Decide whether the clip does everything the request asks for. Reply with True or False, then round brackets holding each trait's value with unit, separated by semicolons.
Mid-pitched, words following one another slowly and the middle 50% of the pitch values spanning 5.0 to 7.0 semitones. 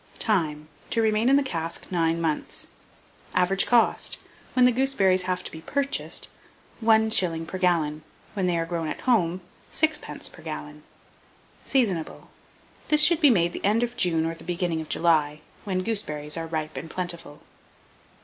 False (180 Hz; 160 wpm; 5.6 semitones)